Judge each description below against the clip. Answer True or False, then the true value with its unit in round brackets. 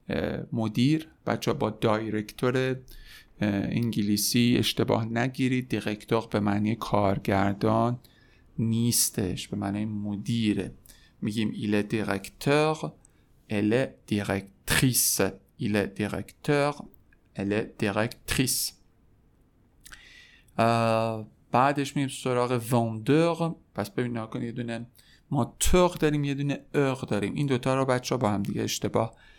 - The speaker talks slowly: True (100 wpm)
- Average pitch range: True (3.6 semitones)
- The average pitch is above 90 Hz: True (115 Hz)